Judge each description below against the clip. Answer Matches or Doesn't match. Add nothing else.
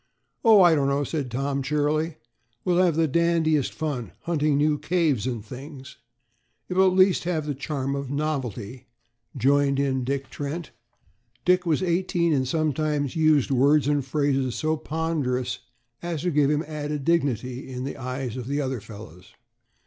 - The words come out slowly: Doesn't match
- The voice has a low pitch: Doesn't match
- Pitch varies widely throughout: Doesn't match